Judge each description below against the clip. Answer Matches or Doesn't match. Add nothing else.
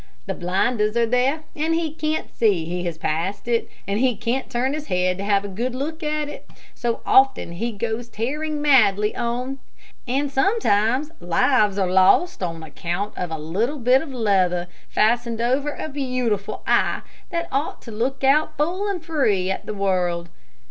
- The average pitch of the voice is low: Doesn't match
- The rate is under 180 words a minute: Doesn't match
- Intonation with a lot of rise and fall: Matches